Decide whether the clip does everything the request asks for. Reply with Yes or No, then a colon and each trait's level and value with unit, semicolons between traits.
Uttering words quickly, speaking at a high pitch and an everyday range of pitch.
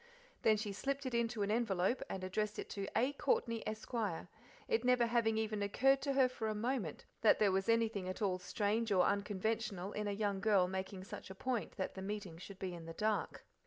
Yes: fast, 215 wpm; high, 210 Hz; average, 3.1 semitones